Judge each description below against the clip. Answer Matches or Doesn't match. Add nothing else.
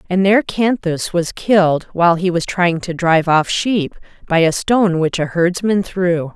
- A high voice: Doesn't match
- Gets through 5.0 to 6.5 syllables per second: Doesn't match